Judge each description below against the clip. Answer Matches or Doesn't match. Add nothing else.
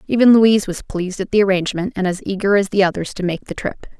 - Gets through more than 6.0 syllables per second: Matches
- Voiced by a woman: Matches